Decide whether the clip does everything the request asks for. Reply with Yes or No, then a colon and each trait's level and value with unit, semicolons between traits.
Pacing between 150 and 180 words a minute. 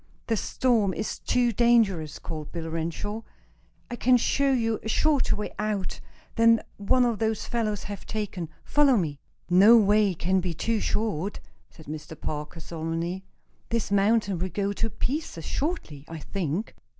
Yes: average, 155 wpm